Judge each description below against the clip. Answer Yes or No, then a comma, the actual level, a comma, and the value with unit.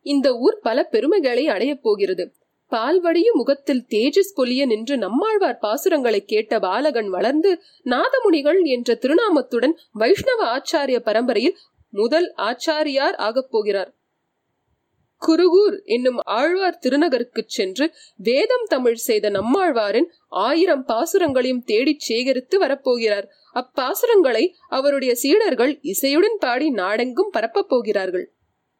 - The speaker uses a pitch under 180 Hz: No, very high, 300 Hz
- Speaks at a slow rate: No, average, 100 wpm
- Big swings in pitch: Yes, wide, 6.5 semitones